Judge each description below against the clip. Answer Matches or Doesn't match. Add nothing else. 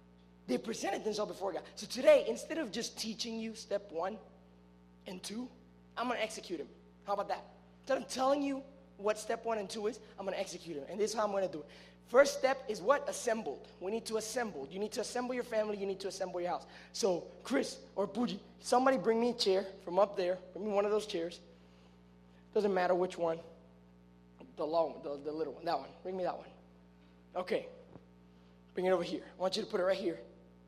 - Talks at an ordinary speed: Doesn't match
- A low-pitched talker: Doesn't match